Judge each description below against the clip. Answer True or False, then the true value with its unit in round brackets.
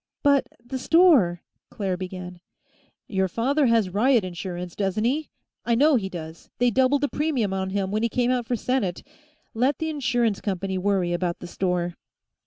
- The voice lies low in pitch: False (210 Hz)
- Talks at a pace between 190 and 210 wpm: False (180 wpm)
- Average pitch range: False (5.7 semitones)